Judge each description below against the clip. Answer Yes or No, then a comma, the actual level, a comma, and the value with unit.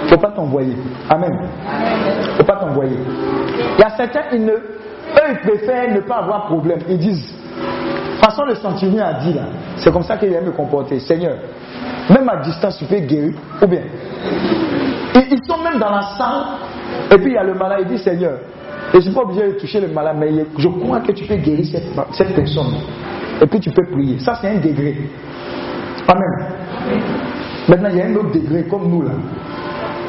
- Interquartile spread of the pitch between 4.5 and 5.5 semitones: Yes, average, 5.1 semitones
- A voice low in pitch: No, medium, 180 Hz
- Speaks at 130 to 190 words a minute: No, average, 210 wpm